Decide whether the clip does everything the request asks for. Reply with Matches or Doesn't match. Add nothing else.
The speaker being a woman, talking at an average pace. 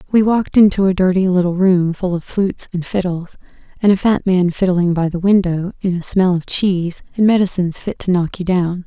Doesn't match